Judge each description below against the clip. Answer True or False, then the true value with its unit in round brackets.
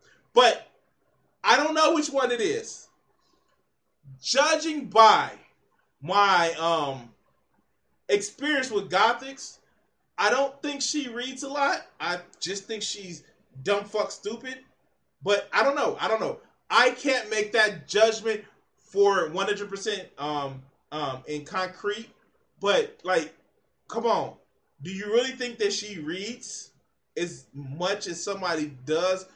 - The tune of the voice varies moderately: False (6.8 semitones)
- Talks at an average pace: False (130 wpm)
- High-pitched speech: True (205 Hz)